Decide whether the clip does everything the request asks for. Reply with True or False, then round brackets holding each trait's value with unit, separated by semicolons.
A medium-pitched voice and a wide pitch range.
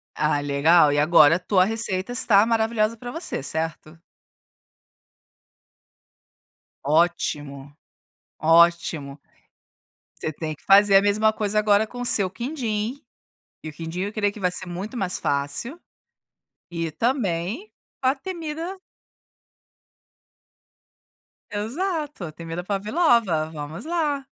False (195 Hz; 6.4 semitones)